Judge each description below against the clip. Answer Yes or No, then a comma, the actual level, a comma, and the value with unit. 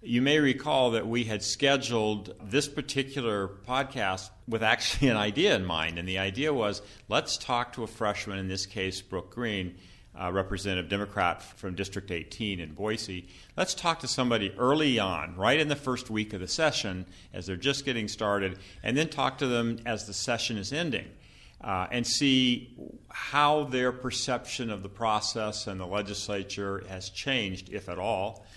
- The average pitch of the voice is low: Yes, low, 105 Hz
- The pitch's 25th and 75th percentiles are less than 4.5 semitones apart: No, average, 4.8 semitones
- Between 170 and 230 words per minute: Yes, average, 175 wpm